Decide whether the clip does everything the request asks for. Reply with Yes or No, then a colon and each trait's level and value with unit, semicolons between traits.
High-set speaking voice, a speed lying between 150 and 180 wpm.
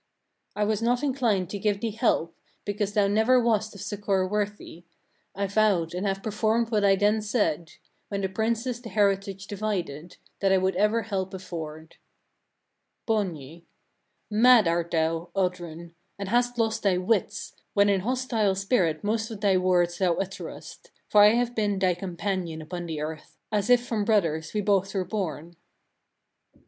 Yes: high, 200 Hz; average, 165 wpm